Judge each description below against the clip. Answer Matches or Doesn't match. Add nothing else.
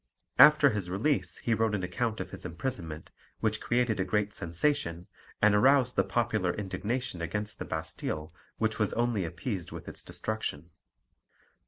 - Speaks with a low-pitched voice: Matches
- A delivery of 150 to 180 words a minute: Matches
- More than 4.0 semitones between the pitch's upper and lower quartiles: Matches